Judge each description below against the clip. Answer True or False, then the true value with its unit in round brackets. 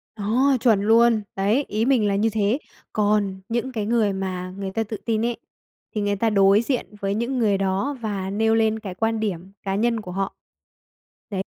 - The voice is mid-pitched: False (215 Hz)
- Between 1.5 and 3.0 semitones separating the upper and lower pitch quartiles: True (2.5 semitones)